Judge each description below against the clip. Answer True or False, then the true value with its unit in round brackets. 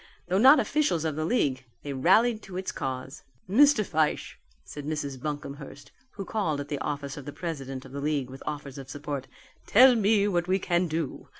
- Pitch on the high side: False (155 Hz)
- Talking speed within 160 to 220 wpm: True (195 wpm)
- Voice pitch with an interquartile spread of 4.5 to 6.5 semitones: True (5.6 semitones)